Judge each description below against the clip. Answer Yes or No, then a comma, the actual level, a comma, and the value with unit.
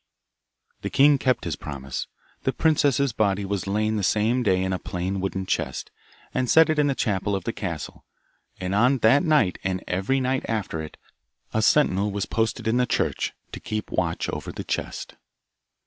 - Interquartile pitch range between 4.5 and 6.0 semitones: Yes, average, 5.2 semitones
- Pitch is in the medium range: No, low, 105 Hz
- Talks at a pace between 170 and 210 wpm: Yes, average, 180 wpm